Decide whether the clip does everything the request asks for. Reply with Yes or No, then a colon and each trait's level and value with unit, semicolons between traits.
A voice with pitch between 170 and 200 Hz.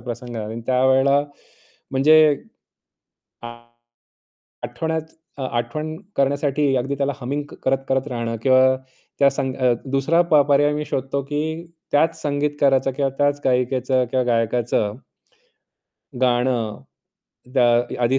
No: low, 135 Hz